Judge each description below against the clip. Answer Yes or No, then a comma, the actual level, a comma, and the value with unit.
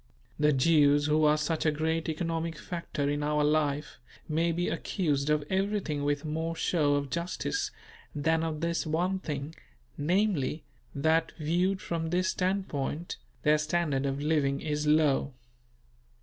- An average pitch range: No, narrow, 2.3 semitones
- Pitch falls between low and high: Yes, medium, 155 Hz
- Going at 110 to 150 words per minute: Yes, average, 145 wpm